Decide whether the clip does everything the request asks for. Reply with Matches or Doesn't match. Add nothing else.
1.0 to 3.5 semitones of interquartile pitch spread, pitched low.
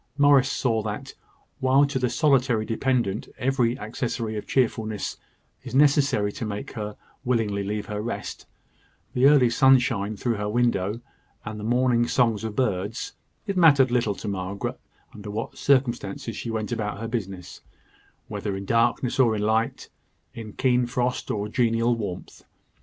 Matches